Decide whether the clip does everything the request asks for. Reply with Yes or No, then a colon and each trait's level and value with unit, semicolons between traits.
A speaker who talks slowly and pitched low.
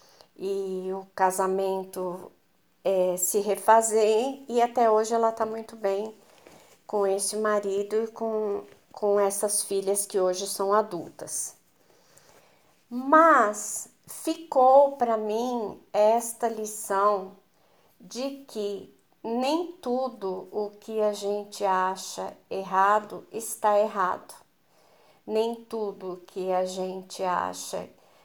No: slow, 105 wpm; high, 210 Hz